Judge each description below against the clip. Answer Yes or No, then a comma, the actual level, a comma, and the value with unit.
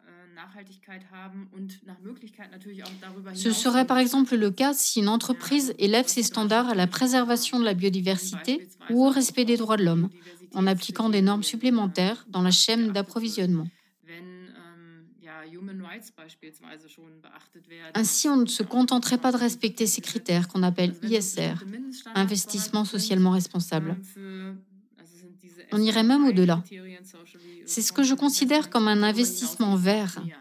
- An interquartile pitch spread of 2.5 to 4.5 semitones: Yes, average, 4.2 semitones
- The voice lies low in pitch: No, high, 200 Hz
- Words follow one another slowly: Yes, slow, 125 wpm